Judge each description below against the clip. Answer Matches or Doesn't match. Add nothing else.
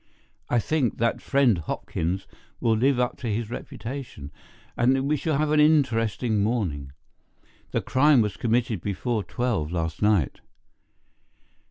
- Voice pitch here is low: Matches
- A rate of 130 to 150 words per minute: Matches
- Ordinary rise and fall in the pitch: Matches